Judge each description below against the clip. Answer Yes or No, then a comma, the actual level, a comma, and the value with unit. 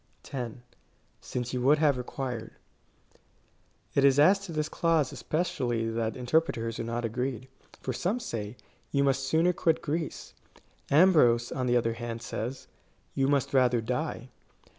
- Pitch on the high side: No, low, 130 Hz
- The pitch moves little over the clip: No, average, 4.3 semitones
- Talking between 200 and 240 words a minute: No, average, 155 wpm